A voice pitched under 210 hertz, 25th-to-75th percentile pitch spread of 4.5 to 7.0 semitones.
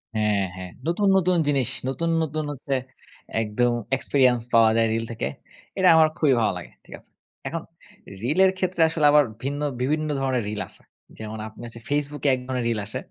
Yes: low, 135 Hz; average, 5.3 semitones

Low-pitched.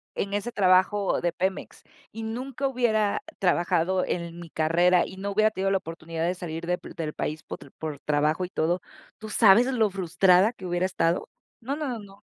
No: medium, 185 Hz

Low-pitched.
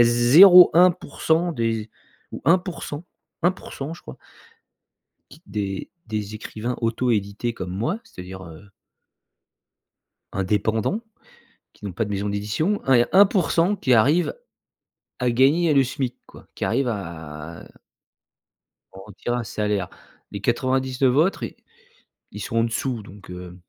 Yes: low, 115 Hz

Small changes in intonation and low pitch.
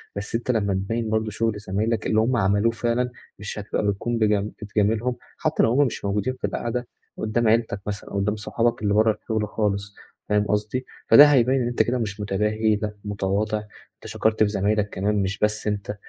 Yes: narrow, 2.0 semitones; low, 105 Hz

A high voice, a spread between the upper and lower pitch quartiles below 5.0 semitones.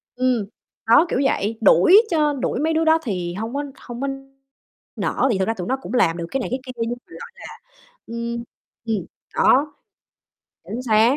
Yes: high, 240 Hz; average, 3.9 semitones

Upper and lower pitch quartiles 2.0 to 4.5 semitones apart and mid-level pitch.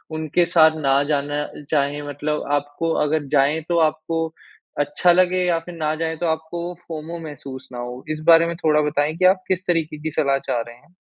Yes: narrow, 2.4 semitones; medium, 155 Hz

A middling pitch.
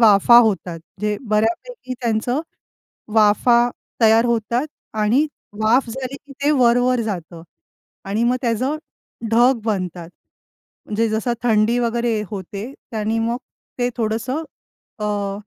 No: high, 230 Hz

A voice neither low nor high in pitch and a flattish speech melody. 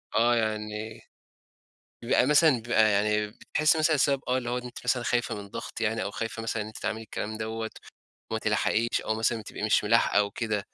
No: low, 110 Hz; narrow, 2.0 semitones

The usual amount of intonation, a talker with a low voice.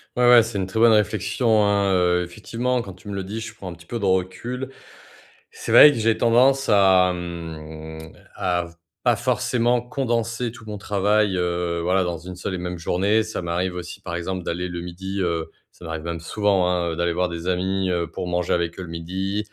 Yes: average, 3.7 semitones; very low, 95 Hz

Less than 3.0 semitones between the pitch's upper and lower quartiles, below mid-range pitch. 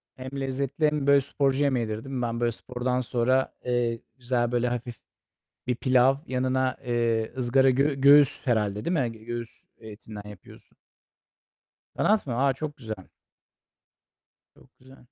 Yes: narrow, 2.4 semitones; low, 125 Hz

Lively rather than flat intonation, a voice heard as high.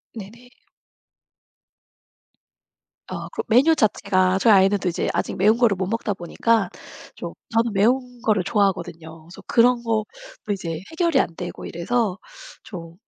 No: average, 4.3 semitones; high, 205 Hz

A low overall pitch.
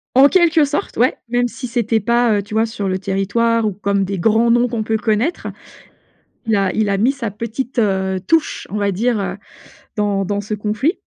No: high, 220 Hz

